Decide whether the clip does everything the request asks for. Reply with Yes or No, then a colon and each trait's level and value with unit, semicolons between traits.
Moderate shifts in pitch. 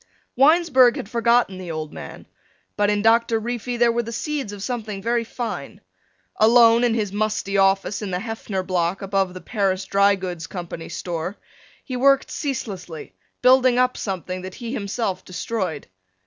Yes: average, 4.1 semitones